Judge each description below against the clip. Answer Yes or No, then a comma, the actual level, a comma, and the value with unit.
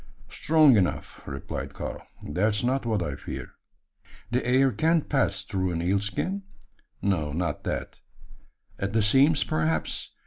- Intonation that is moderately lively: No, wide, 7.2 semitones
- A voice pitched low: Yes, low, 105 Hz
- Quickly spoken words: No, average, 140 wpm